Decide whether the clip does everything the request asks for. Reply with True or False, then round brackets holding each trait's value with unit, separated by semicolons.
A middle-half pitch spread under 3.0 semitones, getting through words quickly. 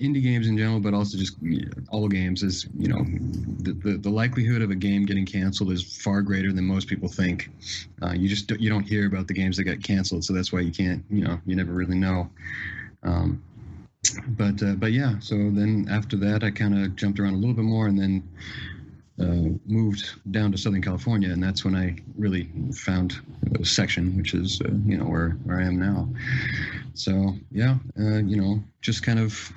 True (2.5 semitones; 210 wpm)